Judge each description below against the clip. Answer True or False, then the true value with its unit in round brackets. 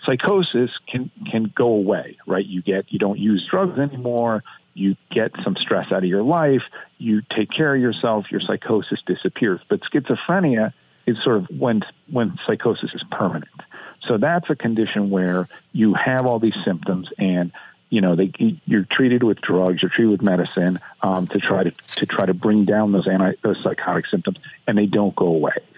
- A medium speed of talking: True (185 wpm)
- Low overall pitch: True (105 Hz)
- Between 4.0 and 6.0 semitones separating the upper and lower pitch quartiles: True (4.6 semitones)